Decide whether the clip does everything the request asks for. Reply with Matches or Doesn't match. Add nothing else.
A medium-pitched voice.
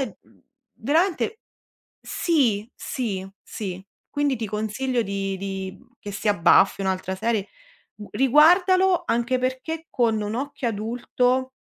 Doesn't match